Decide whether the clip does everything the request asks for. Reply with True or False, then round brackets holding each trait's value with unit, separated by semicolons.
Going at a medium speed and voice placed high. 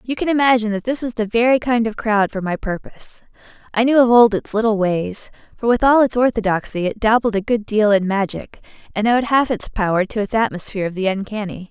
False (225 wpm; 220 Hz)